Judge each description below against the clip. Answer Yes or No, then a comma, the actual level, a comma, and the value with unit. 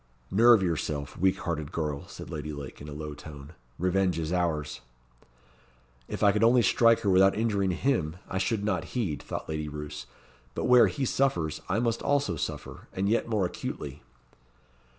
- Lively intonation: Yes, wide, 6.2 semitones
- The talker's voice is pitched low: Yes, very low, 90 Hz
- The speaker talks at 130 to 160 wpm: No, average, 170 wpm